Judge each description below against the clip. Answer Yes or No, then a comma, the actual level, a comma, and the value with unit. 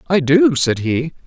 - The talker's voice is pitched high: No, medium, 155 Hz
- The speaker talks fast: No, average, 190 wpm